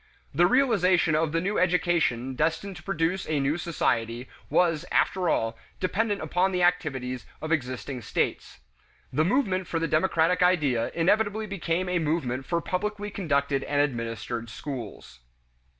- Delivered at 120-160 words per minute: Yes, average, 145 wpm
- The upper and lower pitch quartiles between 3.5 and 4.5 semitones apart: No, average, 5.2 semitones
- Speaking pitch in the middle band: Yes, medium, 165 Hz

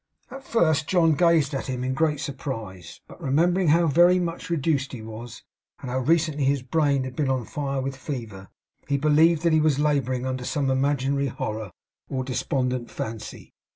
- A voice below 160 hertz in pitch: Yes, medium, 140 Hz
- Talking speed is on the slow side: No, average, 175 wpm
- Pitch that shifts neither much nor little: Yes, average, 3.4 semitones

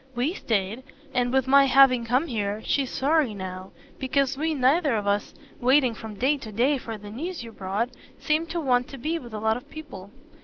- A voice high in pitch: Yes, very high, 250 Hz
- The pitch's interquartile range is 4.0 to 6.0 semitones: Yes, average, 4.3 semitones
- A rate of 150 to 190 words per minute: No, fast, 205 wpm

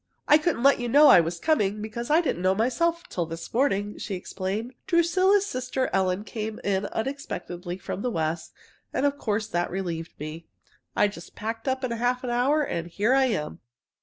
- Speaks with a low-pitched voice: No, high, 220 Hz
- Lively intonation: Yes, wide, 6.3 semitones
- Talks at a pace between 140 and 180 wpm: No, average, 190 wpm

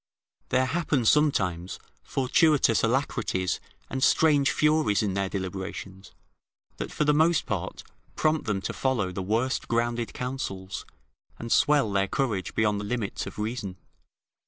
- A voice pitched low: Yes, low, 115 Hz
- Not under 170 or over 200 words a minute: No, slow, 135 wpm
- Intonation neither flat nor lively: No, wide, 6.0 semitones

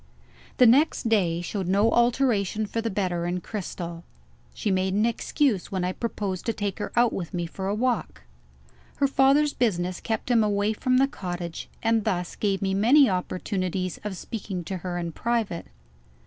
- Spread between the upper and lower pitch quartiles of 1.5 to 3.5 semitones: No, average, 4.1 semitones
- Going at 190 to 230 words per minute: No, average, 175 wpm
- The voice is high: Yes, high, 200 Hz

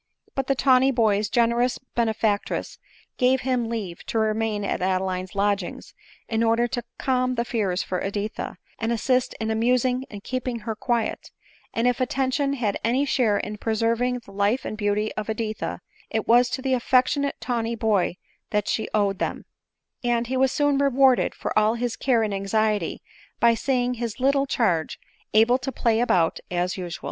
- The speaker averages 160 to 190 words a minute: Yes, average, 170 wpm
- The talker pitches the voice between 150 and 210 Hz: No, high, 230 Hz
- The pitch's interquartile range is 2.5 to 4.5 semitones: Yes, average, 3.2 semitones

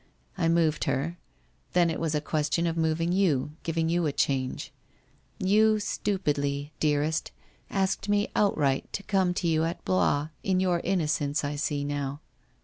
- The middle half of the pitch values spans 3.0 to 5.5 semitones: Yes, average, 3.9 semitones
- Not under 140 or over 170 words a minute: Yes, average, 160 wpm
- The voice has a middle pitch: Yes, medium, 165 Hz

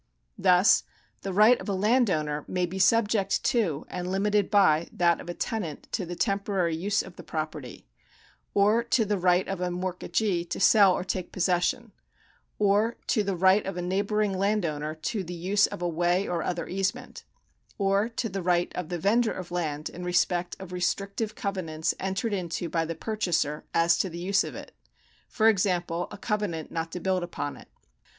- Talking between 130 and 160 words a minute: No, average, 185 wpm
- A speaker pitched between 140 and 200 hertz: Yes, medium, 185 Hz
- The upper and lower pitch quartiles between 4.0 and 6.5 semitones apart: No, average, 2.8 semitones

